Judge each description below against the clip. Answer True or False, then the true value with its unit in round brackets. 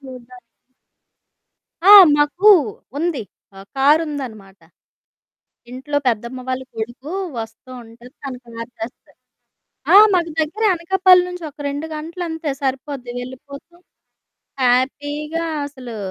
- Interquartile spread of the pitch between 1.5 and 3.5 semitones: False (4.6 semitones)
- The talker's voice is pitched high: True (275 Hz)